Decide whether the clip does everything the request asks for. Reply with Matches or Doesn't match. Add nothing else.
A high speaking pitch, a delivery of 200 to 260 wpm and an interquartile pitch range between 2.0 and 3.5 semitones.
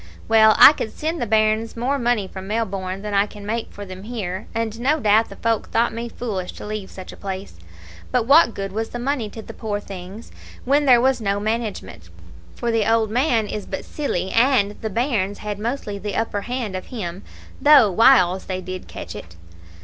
Matches